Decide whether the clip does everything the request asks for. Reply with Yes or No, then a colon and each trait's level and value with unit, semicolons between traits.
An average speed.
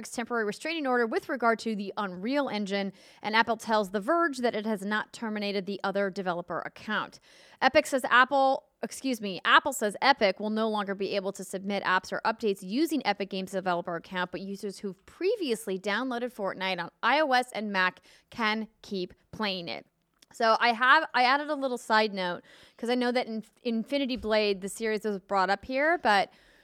Yes: average, 185 wpm